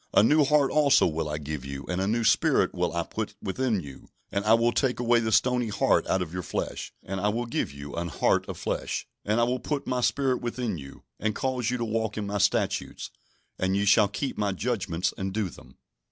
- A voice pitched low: Yes, low, 105 Hz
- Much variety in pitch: No, average, 4.7 semitones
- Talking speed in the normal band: No, fast, 235 wpm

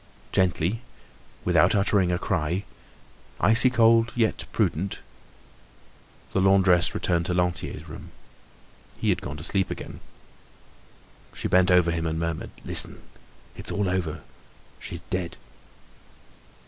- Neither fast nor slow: No, slow, 120 wpm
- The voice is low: Yes, very low, 90 Hz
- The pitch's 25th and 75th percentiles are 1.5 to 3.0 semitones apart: Yes, average, 2.7 semitones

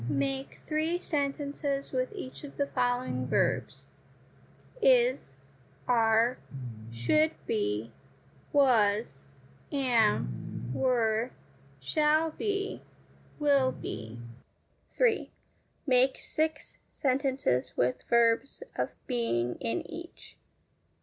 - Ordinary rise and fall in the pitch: No, wide, 5.8 semitones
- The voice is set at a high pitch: Yes, very high, 255 Hz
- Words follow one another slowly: Yes, slow, 85 wpm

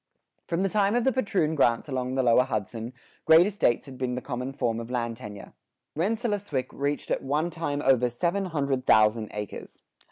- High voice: No, low, 135 Hz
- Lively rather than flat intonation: Yes, wide, 6.0 semitones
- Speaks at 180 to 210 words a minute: Yes, average, 185 wpm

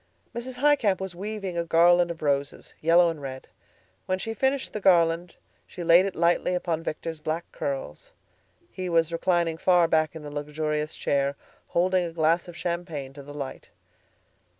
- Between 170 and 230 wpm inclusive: Yes, average, 175 wpm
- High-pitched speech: No, medium, 170 Hz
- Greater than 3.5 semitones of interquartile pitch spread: No, average, 2.9 semitones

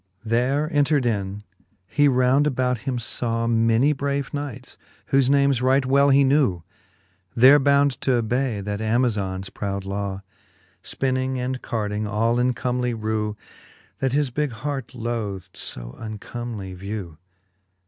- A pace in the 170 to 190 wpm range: No, slow, 135 wpm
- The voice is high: No, low, 120 Hz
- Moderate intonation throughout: Yes, average, 4.1 semitones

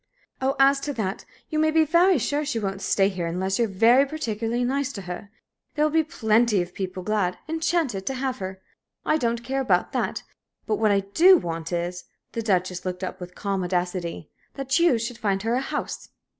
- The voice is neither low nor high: No, high, 225 Hz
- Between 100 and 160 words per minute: No, average, 200 wpm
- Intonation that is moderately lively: No, wide, 6.4 semitones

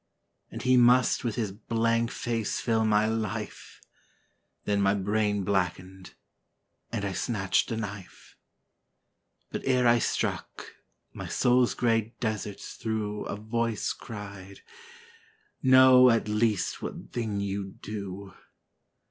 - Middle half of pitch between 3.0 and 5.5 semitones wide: No, narrow, 2.6 semitones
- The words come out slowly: Yes, slow, 120 wpm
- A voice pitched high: No, low, 110 Hz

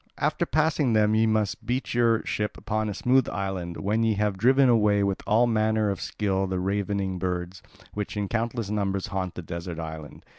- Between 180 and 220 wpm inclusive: Yes, average, 190 wpm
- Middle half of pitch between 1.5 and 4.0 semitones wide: Yes, average, 2.8 semitones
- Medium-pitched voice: No, low, 105 Hz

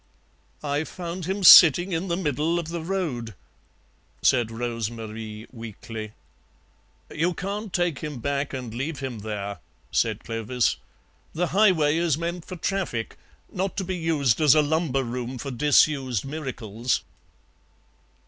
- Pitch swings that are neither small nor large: No, wide, 6.4 semitones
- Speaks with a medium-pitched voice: Yes, medium, 145 Hz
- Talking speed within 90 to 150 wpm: Yes, average, 140 wpm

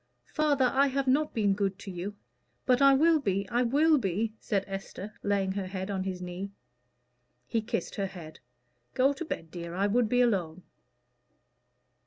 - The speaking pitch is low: No, high, 205 Hz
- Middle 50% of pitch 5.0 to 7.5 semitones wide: Yes, average, 5.3 semitones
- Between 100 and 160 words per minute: No, average, 175 wpm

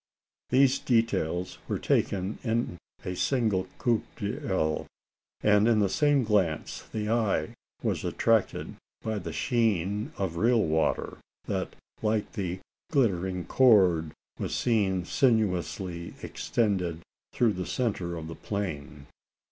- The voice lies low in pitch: Yes, low, 100 Hz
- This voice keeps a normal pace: No, slow, 125 wpm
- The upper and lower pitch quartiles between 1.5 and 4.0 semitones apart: No, average, 4.4 semitones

